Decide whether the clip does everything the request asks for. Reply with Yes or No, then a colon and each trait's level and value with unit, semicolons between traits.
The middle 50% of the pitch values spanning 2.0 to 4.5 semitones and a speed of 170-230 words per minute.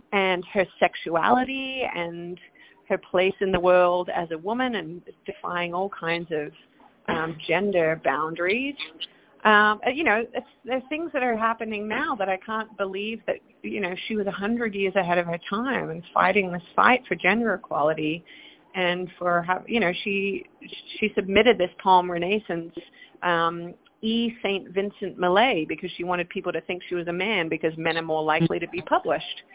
Yes: average, 4.0 semitones; average, 175 wpm